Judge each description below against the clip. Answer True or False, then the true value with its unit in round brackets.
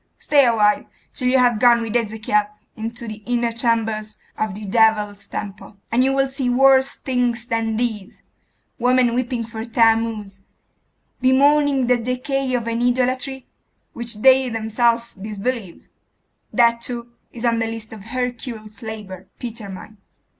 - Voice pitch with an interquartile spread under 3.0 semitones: True (2.4 semitones)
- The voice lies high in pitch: True (235 Hz)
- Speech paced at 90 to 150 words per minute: True (145 wpm)